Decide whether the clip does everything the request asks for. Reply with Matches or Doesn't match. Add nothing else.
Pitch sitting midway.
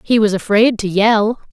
Doesn't match